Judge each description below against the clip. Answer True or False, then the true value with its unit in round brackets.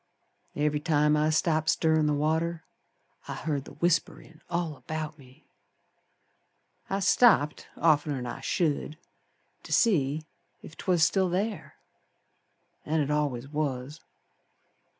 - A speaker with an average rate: False (115 wpm)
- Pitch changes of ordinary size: False (2.0 semitones)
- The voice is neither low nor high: True (155 Hz)